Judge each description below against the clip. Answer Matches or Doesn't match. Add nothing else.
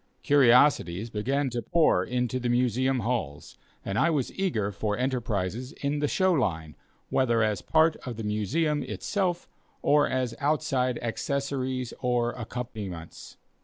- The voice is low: Matches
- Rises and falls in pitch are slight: Doesn't match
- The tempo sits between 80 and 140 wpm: Matches